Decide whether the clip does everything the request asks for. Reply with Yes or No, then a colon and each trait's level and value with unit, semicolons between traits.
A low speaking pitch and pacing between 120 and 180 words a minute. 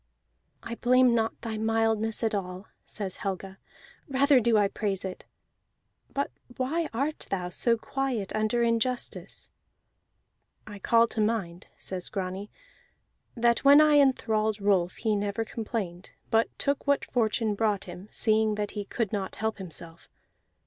No: high, 220 Hz; average, 140 wpm